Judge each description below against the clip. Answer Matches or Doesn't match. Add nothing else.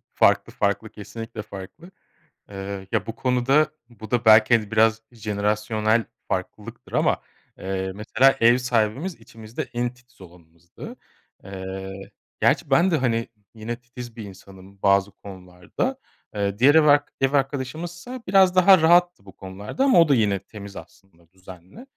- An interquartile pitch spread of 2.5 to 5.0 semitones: Doesn't match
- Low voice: Matches